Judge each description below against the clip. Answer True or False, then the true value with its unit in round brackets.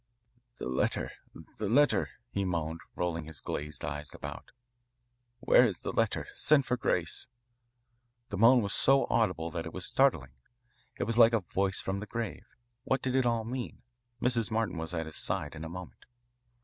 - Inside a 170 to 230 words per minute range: True (175 wpm)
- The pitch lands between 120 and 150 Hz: False (100 Hz)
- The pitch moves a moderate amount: False (6.4 semitones)